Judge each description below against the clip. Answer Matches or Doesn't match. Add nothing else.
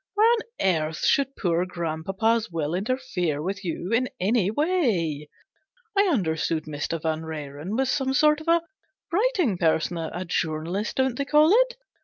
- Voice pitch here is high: Matches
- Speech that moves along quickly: Doesn't match